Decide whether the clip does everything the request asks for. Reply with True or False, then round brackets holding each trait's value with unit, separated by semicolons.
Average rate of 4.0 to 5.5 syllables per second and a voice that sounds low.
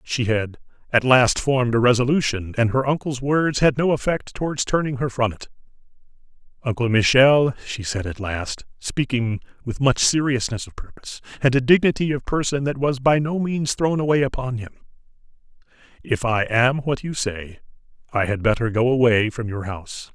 True (5.1 syllables/s; 125 Hz)